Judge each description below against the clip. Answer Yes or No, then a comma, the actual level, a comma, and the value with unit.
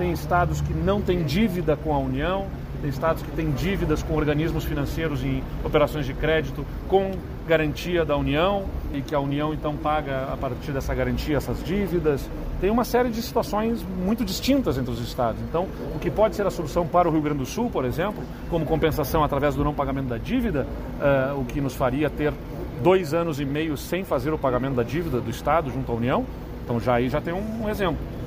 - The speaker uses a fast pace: Yes, fast, 210 wpm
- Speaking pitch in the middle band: Yes, medium, 150 Hz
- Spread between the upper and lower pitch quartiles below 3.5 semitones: No, average, 4.1 semitones